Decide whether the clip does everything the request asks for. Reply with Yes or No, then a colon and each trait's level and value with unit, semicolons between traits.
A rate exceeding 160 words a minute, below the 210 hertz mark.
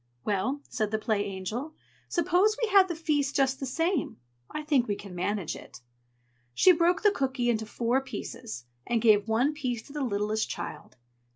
No: average, 180 wpm; very high, 250 Hz